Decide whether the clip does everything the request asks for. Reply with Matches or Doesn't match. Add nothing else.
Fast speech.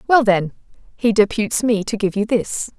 Doesn't match